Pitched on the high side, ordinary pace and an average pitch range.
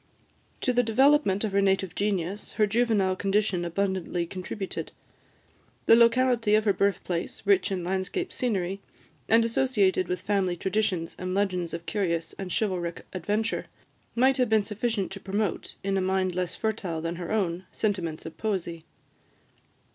Yes: high, 195 Hz; average, 150 wpm; average, 3.2 semitones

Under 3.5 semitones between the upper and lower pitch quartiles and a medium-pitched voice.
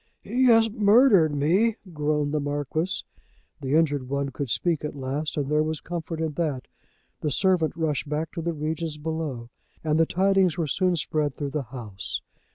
Yes: average, 3.0 semitones; medium, 155 Hz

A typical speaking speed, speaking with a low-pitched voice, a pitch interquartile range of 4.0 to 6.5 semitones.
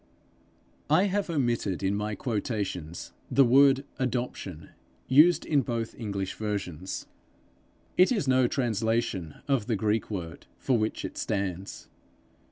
No: slow, 125 wpm; low, 115 Hz; average, 4.9 semitones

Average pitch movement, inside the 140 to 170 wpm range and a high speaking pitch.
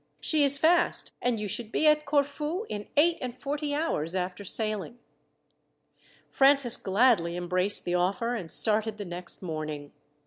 No: wide, 7.7 semitones; average, 150 wpm; high, 220 Hz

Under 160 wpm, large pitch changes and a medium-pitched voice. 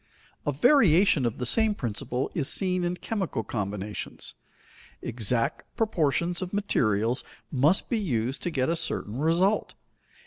Yes: slow, 135 wpm; wide, 7.7 semitones; medium, 155 Hz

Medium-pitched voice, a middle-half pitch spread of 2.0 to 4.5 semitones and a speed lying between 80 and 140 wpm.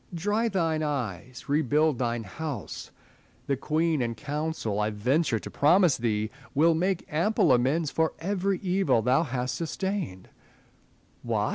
No: medium, 150 Hz; wide, 5.4 semitones; slow, 135 wpm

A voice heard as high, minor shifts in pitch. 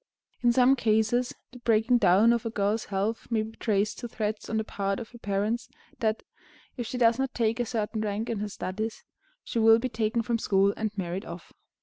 Yes: high, 220 Hz; narrow, 2.1 semitones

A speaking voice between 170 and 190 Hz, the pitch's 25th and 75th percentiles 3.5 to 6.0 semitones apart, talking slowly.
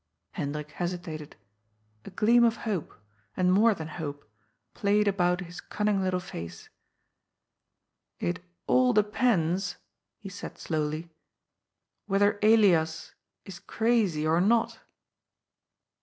Yes: medium, 185 Hz; average, 4.6 semitones; slow, 110 wpm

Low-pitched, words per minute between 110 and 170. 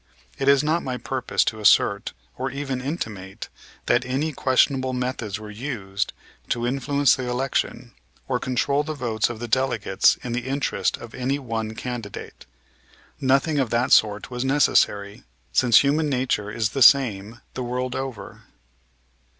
Yes: low, 125 Hz; average, 150 wpm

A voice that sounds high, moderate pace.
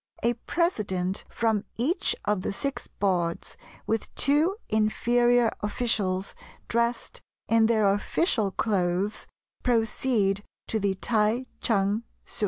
No: high, 220 Hz; slow, 110 wpm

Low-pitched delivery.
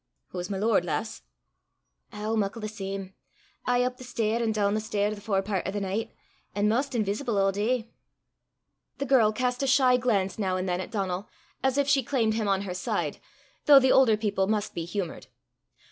No: high, 215 Hz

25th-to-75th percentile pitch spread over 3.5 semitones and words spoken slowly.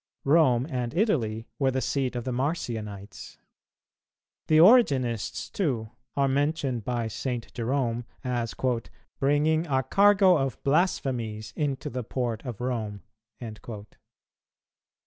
Yes: average, 3.9 semitones; slow, 110 wpm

